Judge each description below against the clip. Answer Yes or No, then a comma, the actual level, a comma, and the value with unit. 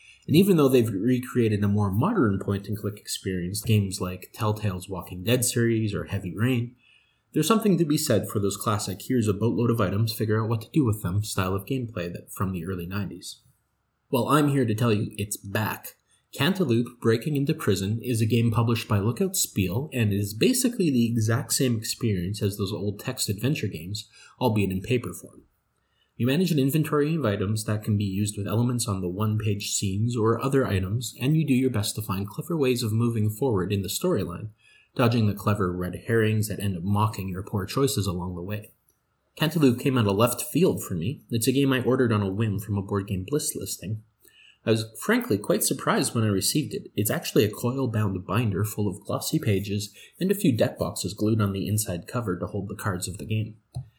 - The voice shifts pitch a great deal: No, average, 3.5 semitones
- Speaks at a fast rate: Yes, fast, 210 wpm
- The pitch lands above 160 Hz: No, low, 110 Hz